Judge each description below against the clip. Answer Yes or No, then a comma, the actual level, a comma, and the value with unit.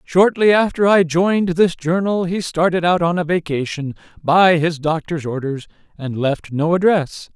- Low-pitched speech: No, medium, 170 Hz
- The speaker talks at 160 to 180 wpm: Yes, average, 165 wpm